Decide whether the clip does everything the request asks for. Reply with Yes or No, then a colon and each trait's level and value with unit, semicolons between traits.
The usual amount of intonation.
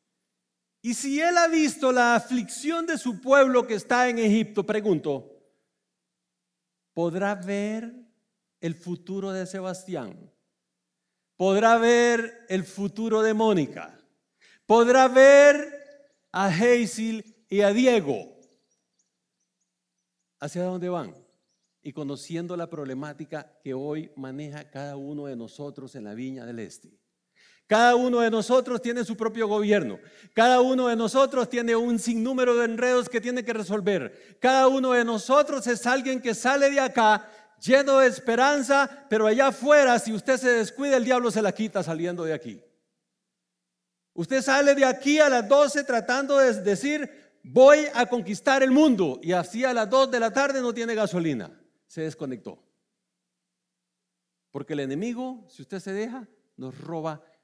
No: wide, 6.9 semitones